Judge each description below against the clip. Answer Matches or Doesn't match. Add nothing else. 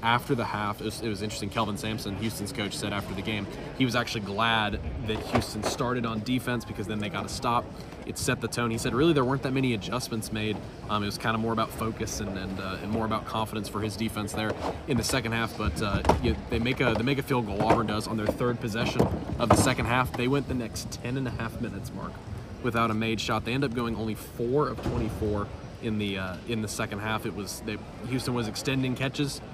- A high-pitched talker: Doesn't match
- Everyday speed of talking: Doesn't match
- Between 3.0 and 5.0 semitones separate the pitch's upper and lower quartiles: Doesn't match